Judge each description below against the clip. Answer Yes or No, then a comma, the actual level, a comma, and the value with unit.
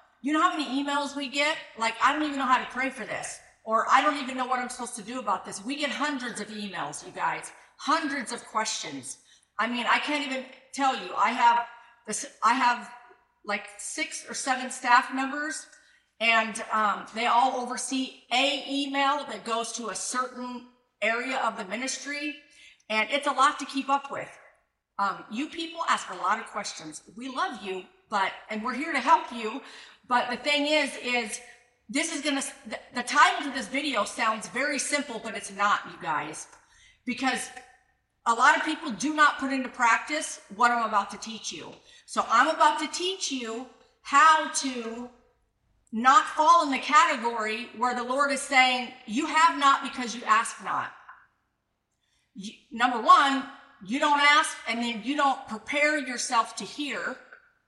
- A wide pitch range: No, average, 4.2 semitones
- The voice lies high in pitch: Yes, very high, 255 Hz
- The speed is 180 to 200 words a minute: Yes, average, 185 wpm